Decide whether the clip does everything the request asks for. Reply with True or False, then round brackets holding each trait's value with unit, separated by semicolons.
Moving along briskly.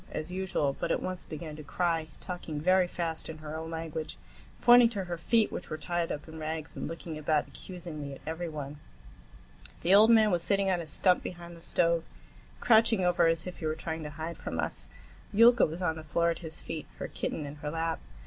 True (220 wpm)